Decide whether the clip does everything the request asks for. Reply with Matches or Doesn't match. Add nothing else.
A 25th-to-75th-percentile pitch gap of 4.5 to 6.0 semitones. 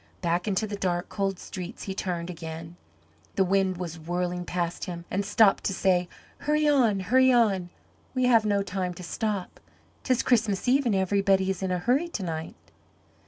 Doesn't match